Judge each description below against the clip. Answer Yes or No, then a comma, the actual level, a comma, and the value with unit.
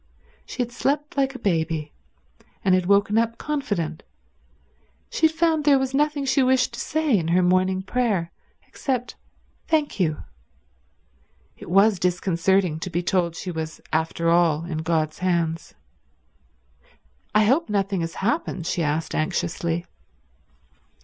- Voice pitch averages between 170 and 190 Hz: Yes, medium, 185 Hz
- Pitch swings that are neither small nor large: No, wide, 7.3 semitones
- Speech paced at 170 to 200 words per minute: No, average, 140 wpm